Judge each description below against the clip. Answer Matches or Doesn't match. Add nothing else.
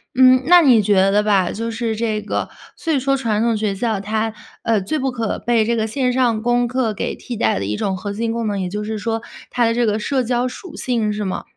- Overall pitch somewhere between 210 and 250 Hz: Matches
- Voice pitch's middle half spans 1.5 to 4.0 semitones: Matches